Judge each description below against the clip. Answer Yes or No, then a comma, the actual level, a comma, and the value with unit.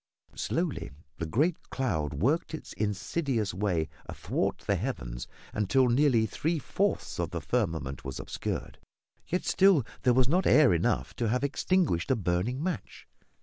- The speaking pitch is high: No, low, 120 Hz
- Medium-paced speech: Yes, average, 145 wpm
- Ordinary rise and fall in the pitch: No, wide, 8.9 semitones